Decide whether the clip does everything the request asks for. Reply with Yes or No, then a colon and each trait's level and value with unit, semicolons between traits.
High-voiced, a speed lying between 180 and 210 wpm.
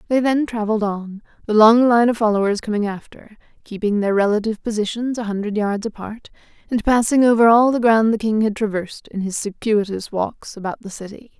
Yes: high, 215 Hz; average, 190 wpm